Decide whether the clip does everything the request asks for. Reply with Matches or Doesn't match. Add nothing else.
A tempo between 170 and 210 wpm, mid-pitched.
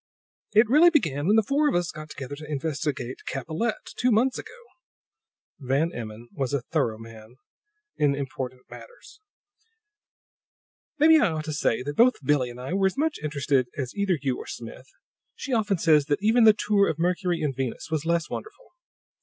Matches